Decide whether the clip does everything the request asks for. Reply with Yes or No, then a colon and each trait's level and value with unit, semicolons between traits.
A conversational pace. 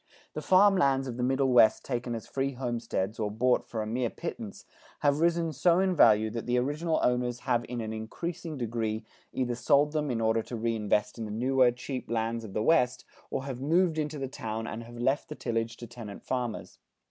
No: fast, 210 wpm